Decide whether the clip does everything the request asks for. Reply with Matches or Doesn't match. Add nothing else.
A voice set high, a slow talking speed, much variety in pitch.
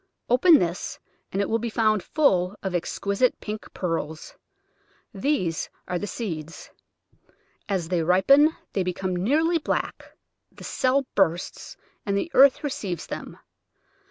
Matches